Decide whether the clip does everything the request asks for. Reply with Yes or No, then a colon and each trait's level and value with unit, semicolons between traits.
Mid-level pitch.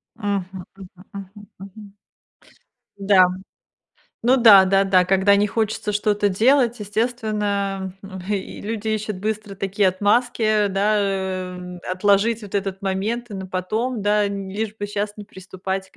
No: high, 200 Hz